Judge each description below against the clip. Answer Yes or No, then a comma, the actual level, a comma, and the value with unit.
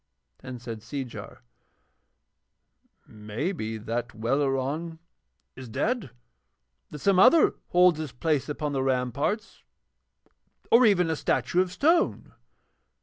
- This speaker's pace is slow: Yes, slow, 110 wpm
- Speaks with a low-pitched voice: No, medium, 145 Hz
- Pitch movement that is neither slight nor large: No, wide, 6.7 semitones